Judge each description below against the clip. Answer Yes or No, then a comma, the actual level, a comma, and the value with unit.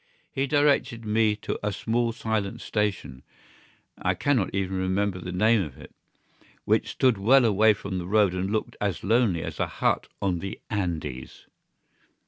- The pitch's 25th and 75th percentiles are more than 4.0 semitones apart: No, average, 3.3 semitones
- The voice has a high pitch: No, low, 105 Hz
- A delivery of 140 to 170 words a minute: Yes, average, 160 wpm